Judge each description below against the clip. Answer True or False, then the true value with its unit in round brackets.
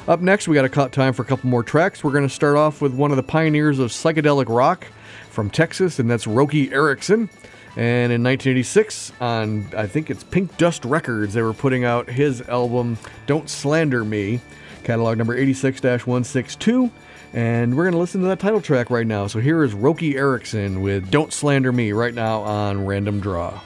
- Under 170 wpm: False (200 wpm)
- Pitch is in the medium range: False (130 Hz)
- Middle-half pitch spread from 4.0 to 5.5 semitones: True (4.5 semitones)